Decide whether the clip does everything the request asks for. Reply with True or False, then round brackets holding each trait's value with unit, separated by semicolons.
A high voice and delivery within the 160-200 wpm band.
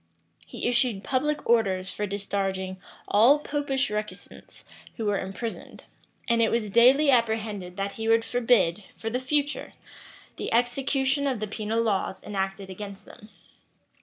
False (225 Hz; 140 wpm)